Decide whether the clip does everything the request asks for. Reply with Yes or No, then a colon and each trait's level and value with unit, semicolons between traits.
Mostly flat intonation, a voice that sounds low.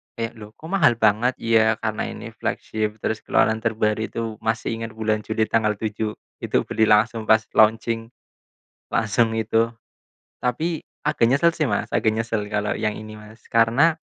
Yes: narrow, 1.1 semitones; low, 110 Hz